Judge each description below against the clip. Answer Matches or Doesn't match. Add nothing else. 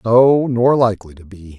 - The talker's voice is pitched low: Matches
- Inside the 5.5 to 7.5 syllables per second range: Doesn't match